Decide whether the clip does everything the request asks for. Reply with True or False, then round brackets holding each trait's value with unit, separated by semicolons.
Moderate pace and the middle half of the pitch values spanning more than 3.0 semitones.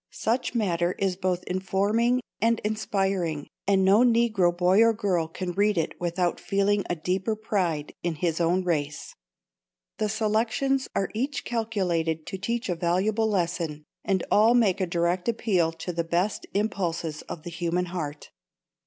True (155 wpm; 4.0 semitones)